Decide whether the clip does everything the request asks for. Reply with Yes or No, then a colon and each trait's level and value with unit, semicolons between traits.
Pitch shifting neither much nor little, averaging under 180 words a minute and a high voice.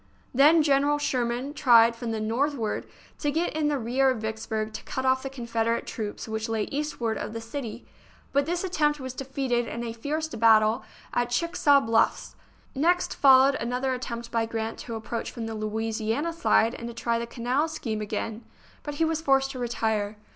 No: average, 3.9 semitones; average, 190 wpm; high, 240 Hz